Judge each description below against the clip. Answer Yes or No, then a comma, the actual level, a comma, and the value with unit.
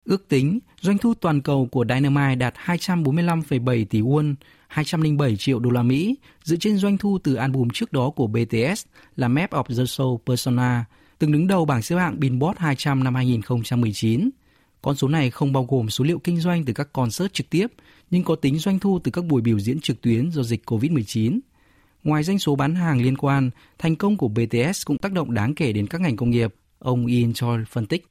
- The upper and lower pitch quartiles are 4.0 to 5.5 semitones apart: Yes, average, 5.2 semitones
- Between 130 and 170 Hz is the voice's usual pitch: Yes, medium, 140 Hz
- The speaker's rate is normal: Yes, average, 210 wpm